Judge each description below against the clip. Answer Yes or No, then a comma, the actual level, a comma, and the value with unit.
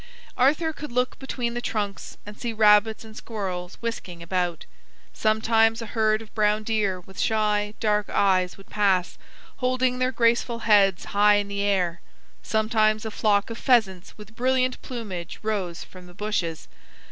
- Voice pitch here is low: No, high, 215 Hz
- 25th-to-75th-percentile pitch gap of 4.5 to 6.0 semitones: No, average, 2.8 semitones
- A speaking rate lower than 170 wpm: Yes, average, 160 wpm